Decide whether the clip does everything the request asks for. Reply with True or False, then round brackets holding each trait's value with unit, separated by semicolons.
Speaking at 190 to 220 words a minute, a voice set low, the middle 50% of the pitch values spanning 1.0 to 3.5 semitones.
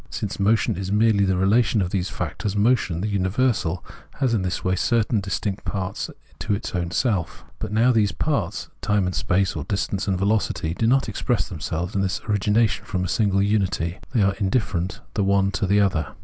True (195 wpm; 100 Hz; 2.6 semitones)